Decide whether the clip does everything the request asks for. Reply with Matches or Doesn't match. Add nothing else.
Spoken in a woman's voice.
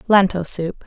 Matches